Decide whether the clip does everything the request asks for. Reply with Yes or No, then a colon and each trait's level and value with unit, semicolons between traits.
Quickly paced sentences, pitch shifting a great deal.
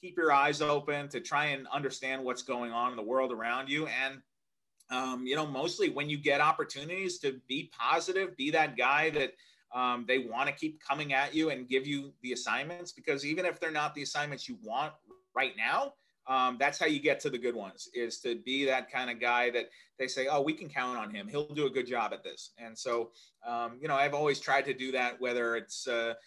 No: fast, 230 wpm; average, 3.8 semitones